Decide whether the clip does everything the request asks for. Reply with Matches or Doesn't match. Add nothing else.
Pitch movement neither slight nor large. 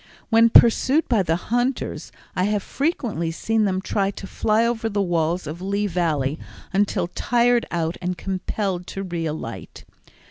Matches